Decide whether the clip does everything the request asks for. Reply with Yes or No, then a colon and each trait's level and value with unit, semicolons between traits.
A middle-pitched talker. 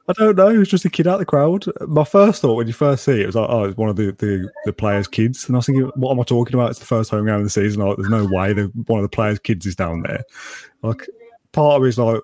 No: low, 115 Hz